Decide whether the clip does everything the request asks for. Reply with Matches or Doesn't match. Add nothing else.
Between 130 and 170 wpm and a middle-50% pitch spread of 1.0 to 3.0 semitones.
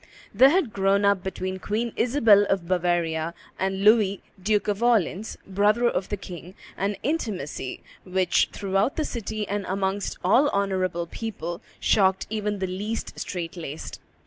Matches